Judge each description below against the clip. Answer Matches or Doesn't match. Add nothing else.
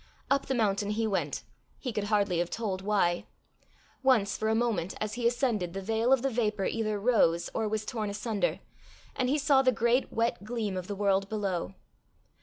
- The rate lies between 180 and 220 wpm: Matches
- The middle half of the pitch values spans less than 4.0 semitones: Matches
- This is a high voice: Matches